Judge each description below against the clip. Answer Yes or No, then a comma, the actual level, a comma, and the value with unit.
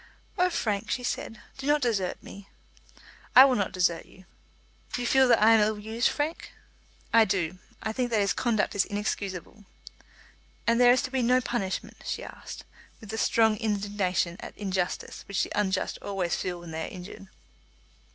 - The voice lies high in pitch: Yes, high, 210 Hz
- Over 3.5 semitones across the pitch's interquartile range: Yes, average, 4.1 semitones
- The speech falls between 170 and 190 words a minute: Yes, average, 180 wpm